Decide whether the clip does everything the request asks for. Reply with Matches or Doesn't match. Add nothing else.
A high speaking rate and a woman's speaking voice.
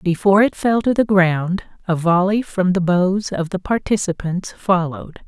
Doesn't match